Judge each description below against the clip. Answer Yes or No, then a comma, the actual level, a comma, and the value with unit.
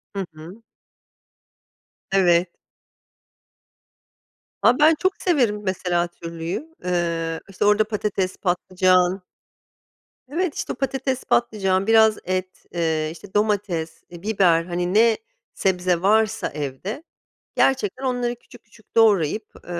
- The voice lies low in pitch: No, high, 195 Hz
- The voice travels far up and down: No, average, 4.2 semitones